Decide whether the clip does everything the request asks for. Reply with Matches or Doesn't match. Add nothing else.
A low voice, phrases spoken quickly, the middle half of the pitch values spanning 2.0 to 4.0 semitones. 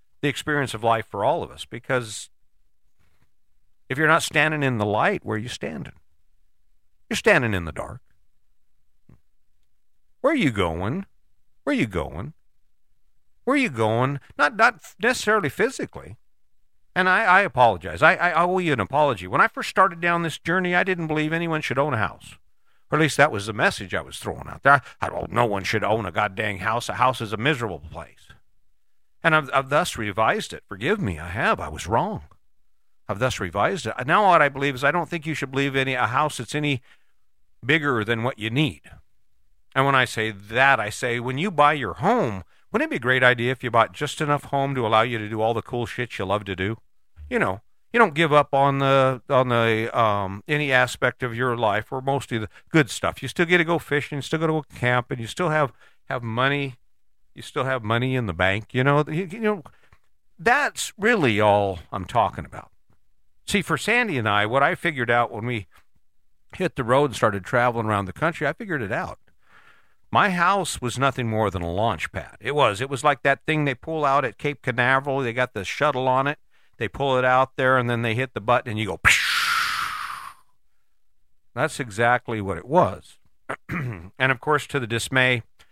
Doesn't match